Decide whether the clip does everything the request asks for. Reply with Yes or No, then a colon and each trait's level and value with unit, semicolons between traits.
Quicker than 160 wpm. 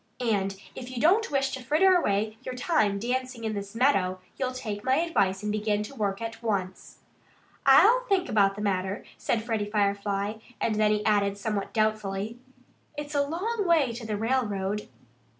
Yes: average, 175 wpm